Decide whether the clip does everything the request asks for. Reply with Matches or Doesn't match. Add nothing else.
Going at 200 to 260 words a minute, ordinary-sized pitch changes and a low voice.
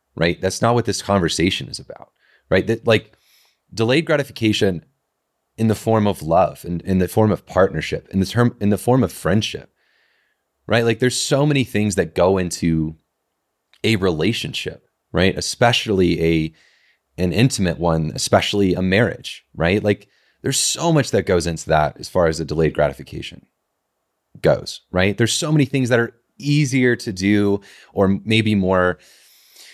Doesn't match